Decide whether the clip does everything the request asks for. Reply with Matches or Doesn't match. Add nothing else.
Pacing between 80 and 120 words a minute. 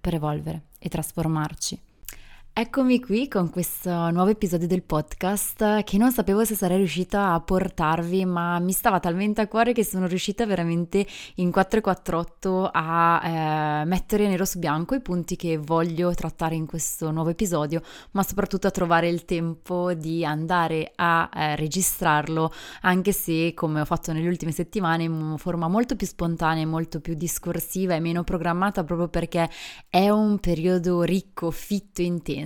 Doesn't match